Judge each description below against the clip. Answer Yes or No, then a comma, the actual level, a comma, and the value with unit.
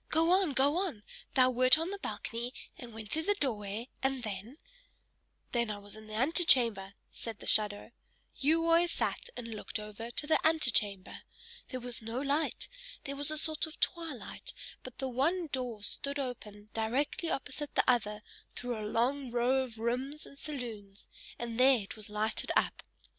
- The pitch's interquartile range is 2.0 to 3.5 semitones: No, average, 4.8 semitones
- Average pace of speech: Yes, average, 180 wpm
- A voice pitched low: No, very high, 250 Hz